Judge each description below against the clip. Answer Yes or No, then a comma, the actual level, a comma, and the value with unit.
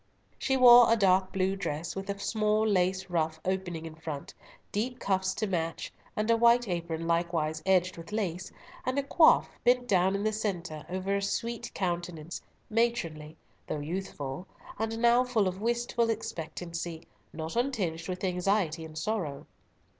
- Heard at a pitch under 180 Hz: No, high, 190 Hz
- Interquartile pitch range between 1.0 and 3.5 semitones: No, average, 4.7 semitones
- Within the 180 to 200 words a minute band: No, average, 160 wpm